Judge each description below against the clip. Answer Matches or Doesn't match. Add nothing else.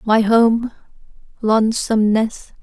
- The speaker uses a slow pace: Matches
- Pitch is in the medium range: Doesn't match